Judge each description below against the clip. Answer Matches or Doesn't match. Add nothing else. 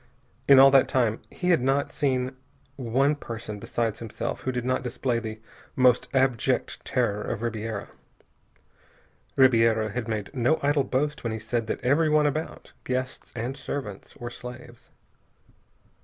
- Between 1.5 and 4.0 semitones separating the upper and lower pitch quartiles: Matches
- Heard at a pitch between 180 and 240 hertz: Doesn't match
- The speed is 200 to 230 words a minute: Doesn't match